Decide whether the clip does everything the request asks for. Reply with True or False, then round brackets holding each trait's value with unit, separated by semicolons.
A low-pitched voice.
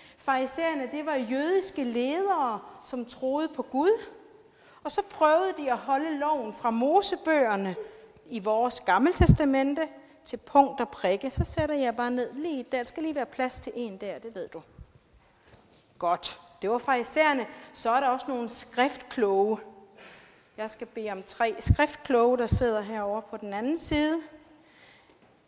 False (260 Hz)